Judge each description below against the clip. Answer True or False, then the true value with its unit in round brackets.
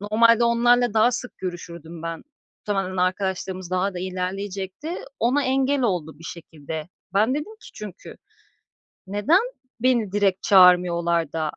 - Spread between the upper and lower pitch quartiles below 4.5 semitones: False (4.8 semitones)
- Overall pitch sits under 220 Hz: True (190 Hz)